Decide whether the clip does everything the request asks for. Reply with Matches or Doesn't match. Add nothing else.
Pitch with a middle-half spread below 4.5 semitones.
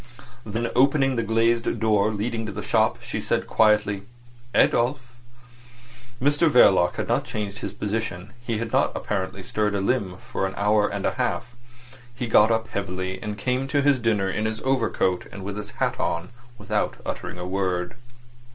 Matches